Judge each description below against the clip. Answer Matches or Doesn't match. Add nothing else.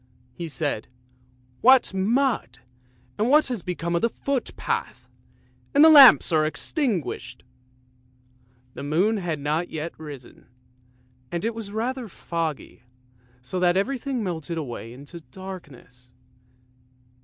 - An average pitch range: Doesn't match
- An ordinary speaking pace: Doesn't match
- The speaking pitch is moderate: Matches